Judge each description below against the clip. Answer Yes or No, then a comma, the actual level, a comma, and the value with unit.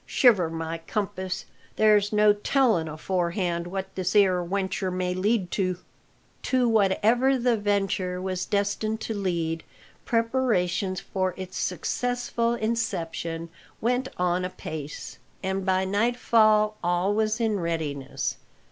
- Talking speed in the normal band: No, slow, 120 wpm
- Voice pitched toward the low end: No, high, 195 Hz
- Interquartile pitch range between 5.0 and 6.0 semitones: No, average, 3.4 semitones